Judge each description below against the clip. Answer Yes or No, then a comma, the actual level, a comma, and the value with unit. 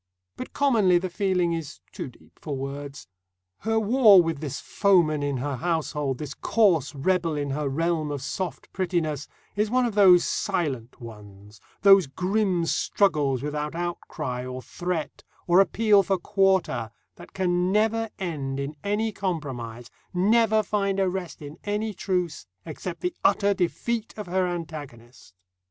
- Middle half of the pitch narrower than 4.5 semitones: No, wide, 5.5 semitones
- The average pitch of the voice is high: No, medium, 175 Hz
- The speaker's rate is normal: Yes, average, 150 wpm